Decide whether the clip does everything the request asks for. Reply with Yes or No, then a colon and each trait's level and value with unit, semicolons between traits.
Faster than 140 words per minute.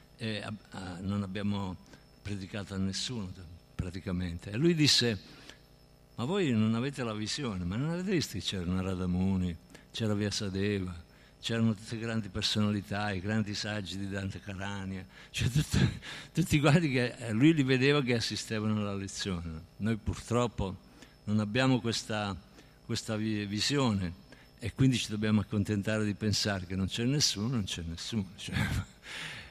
Yes: average, 150 wpm